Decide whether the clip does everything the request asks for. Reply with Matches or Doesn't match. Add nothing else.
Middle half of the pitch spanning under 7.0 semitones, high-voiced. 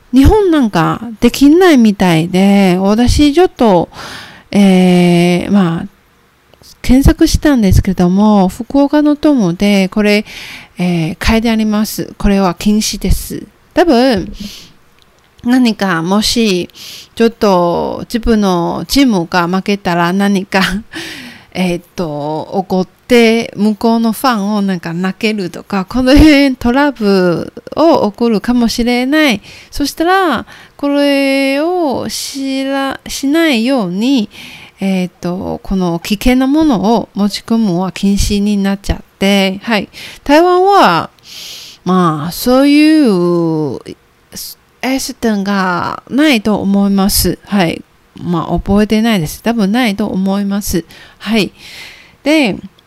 Matches